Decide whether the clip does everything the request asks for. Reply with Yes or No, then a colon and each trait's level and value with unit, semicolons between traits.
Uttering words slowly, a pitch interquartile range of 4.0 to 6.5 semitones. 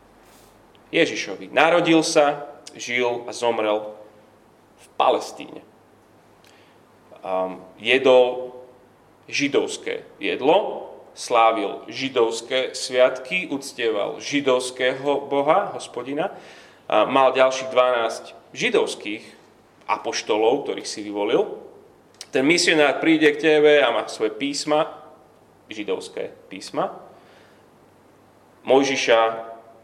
Yes: slow, 75 wpm; average, 5.0 semitones